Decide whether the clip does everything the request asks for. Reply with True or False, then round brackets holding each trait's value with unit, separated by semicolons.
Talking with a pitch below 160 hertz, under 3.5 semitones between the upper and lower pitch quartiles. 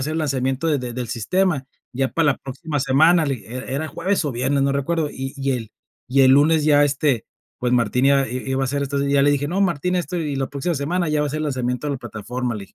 True (140 Hz; 2.9 semitones)